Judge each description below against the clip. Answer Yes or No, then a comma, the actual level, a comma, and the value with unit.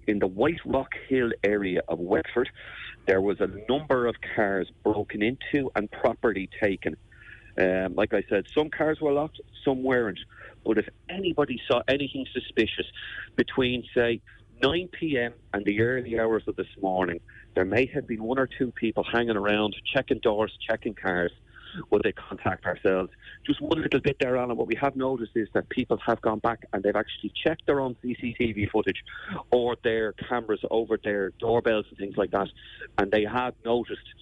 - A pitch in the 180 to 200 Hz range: No, low, 115 Hz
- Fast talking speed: No, average, 180 wpm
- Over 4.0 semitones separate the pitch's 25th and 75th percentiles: No, average, 3.5 semitones